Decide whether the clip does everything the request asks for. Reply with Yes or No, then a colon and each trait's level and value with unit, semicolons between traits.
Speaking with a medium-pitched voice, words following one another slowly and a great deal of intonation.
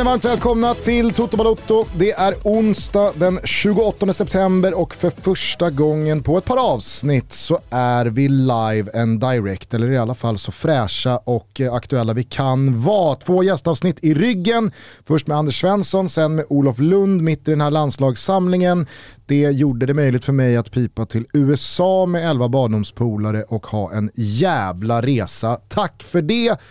No: medium, 145 Hz; average, 160 wpm; wide, 7.6 semitones